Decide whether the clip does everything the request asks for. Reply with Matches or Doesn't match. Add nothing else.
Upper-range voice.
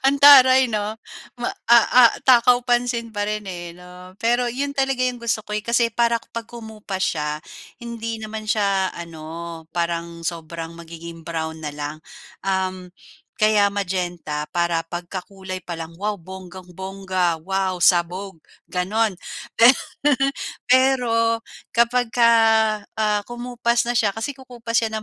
Matches